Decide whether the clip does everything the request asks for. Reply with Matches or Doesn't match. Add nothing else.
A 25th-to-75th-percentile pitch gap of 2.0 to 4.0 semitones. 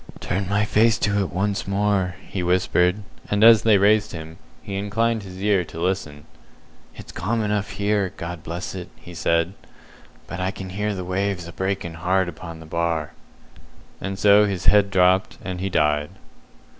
Matches